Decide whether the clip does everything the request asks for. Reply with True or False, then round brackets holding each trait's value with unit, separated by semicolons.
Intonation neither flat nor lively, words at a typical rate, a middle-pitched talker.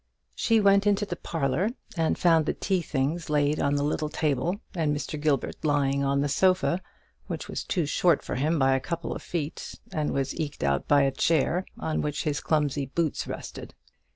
True (3.2 semitones; 195 wpm; 150 Hz)